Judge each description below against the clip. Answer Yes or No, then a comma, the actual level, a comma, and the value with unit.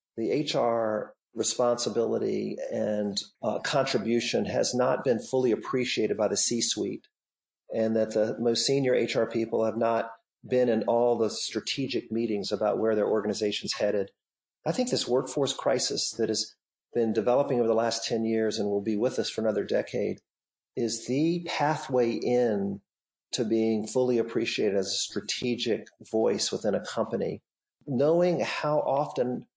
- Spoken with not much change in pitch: Yes, narrow, 2.2 semitones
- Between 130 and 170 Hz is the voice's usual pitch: No, low, 115 Hz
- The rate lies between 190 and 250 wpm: No, average, 150 wpm